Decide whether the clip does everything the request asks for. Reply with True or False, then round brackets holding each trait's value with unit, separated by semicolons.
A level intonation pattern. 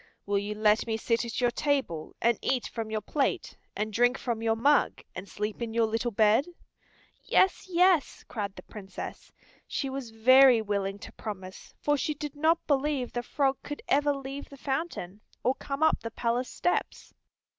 False (4.4 semitones)